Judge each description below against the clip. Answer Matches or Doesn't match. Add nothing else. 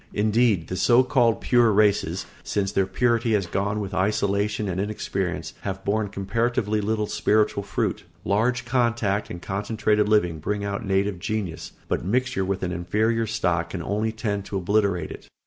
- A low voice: Matches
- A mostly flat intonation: Matches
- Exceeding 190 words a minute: Doesn't match